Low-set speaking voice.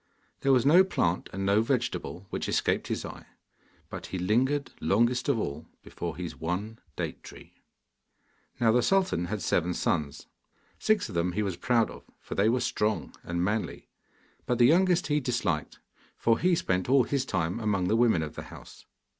Yes: low, 110 Hz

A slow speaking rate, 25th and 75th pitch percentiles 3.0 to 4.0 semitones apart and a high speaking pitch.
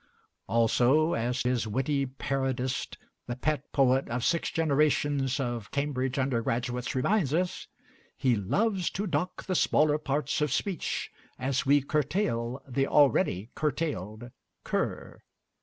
No: slow, 125 wpm; average, 3.5 semitones; low, 135 Hz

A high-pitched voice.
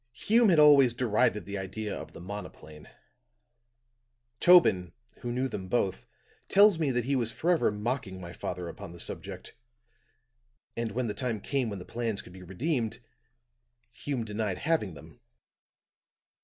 No: low, 115 Hz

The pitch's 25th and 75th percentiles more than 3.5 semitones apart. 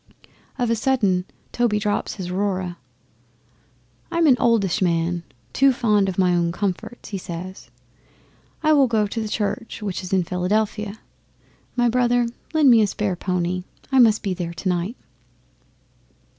Yes: average, 4.4 semitones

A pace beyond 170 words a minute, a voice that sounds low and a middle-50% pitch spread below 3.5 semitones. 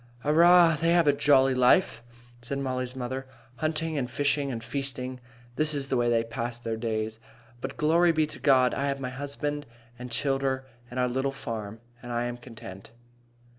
Yes: average, 180 wpm; low, 130 Hz; average, 3.1 semitones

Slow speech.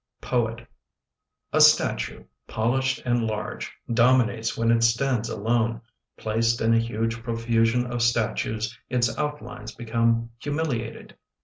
Yes: slow, 115 wpm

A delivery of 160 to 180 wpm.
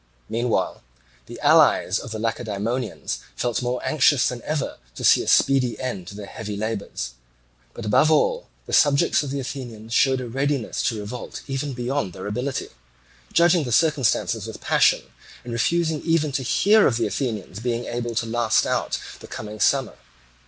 Yes: average, 175 wpm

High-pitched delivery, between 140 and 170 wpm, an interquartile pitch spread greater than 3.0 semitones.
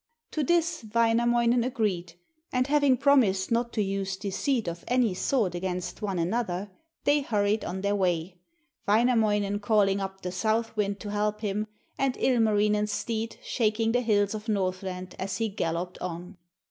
Yes: high, 210 Hz; average, 155 wpm; average, 3.4 semitones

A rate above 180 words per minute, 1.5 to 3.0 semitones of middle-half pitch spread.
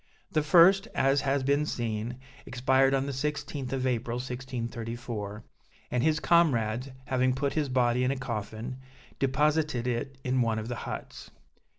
No: average, 155 wpm; average, 2.7 semitones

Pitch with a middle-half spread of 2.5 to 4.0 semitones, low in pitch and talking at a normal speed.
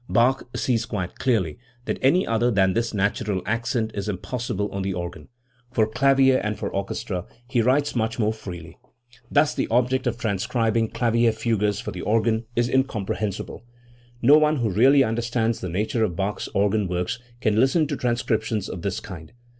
Yes: average, 3.4 semitones; low, 110 Hz; average, 170 wpm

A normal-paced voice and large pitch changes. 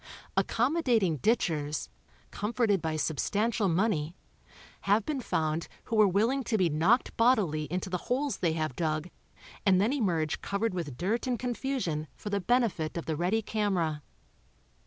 Yes: average, 150 wpm; wide, 6.1 semitones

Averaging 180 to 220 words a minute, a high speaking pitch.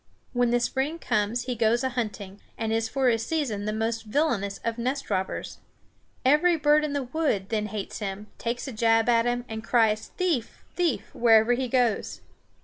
Yes: average, 185 wpm; high, 235 Hz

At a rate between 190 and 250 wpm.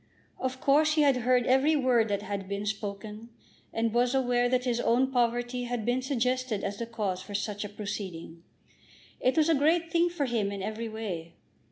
Yes: average, 195 wpm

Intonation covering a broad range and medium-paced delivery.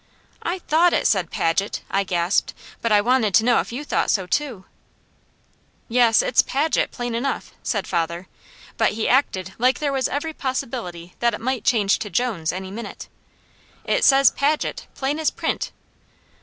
Yes: wide, 5.8 semitones; average, 170 wpm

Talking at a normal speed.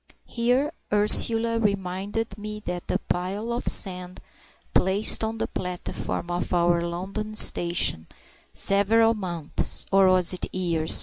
No: slow, 125 wpm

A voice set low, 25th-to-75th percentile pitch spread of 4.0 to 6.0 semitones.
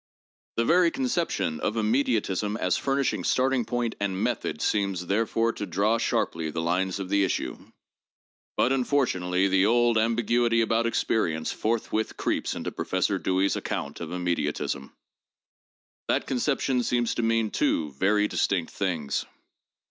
Yes: low, 105 Hz; average, 4.4 semitones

